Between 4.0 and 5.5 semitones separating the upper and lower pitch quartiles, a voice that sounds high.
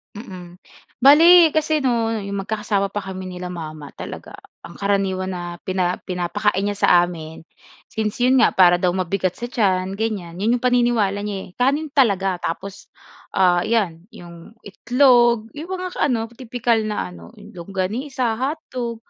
Yes: average, 4.9 semitones; high, 200 Hz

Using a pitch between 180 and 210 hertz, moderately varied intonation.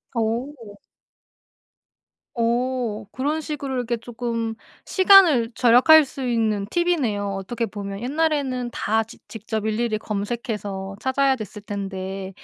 No: high, 230 Hz; average, 3.8 semitones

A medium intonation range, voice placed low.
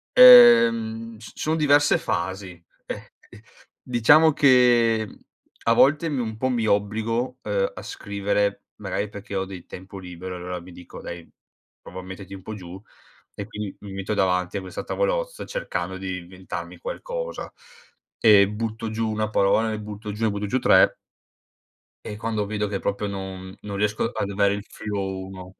Yes: average, 3.1 semitones; low, 105 Hz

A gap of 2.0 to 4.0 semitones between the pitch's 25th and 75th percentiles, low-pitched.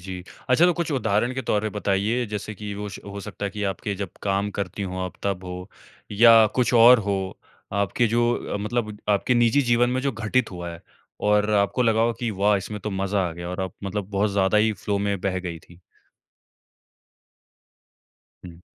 Yes: average, 2.9 semitones; low, 105 Hz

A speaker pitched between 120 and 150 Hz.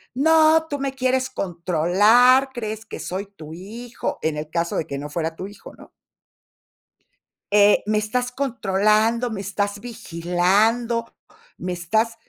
No: high, 210 Hz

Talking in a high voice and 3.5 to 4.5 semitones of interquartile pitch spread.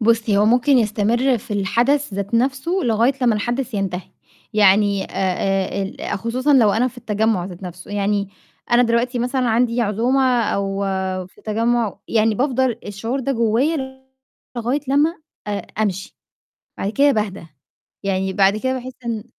Yes: high, 225 Hz; average, 3.9 semitones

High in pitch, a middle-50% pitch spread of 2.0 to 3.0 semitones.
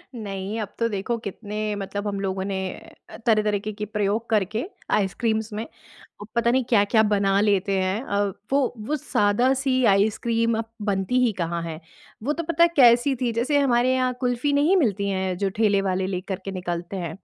No: high, 210 Hz; average, 3.5 semitones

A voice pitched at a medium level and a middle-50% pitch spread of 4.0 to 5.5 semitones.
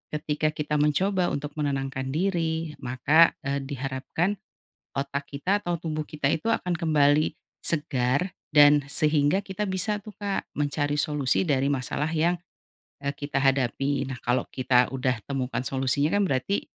No: medium, 145 Hz; average, 3.4 semitones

